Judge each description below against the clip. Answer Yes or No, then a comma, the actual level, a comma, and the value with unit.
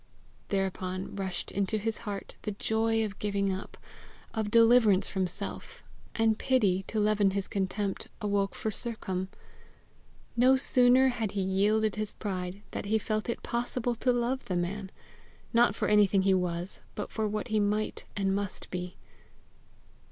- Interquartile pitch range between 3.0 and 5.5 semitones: No, narrow, 2.5 semitones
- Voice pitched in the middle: No, high, 205 Hz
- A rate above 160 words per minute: No, average, 155 wpm